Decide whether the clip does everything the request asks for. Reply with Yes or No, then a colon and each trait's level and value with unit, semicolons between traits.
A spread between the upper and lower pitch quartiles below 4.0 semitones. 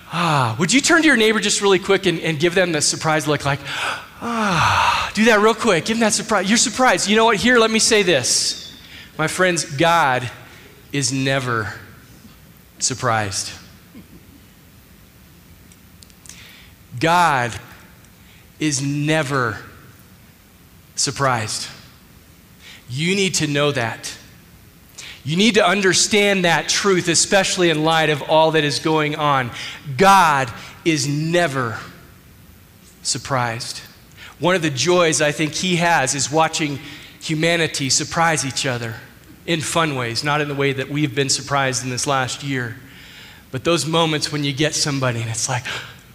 No: average, 5.3 semitones